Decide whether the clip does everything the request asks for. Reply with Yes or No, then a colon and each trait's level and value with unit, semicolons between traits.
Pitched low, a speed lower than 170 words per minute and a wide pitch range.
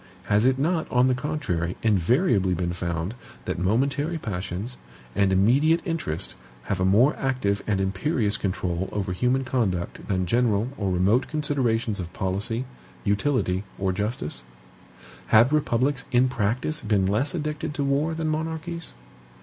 Yes: low, 115 Hz; average, 140 wpm; wide, 6.6 semitones